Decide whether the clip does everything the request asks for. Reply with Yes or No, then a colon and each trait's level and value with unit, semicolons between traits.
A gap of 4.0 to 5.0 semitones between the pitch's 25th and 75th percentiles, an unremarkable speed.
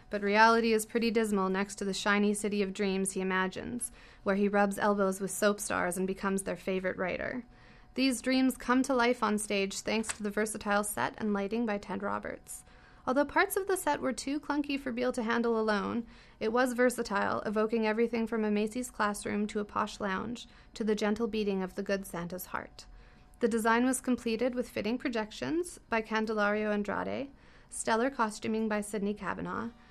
No: average, 2.7 semitones; average, 185 wpm